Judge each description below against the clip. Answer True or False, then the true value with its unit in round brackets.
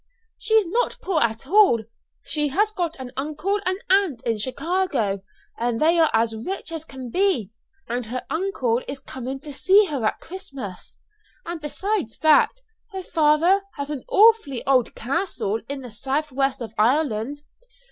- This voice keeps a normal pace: True (165 wpm)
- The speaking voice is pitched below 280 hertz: False (290 Hz)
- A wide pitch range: True (7.1 semitones)